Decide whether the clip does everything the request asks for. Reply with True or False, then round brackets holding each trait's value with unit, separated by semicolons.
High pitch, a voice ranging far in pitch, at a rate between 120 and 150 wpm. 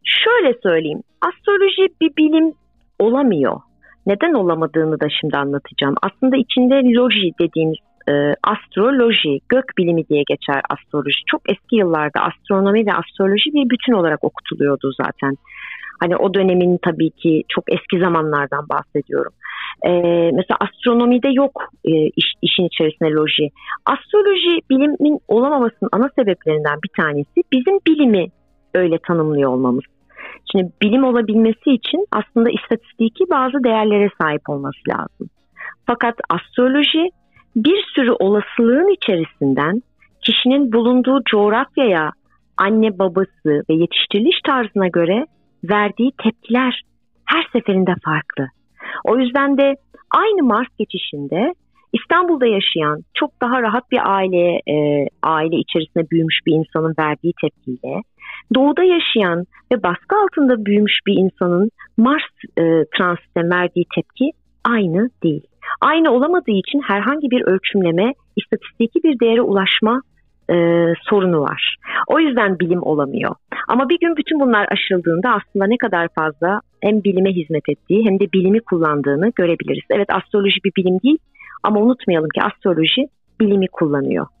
True (200 Hz; 7.1 semitones; 125 wpm)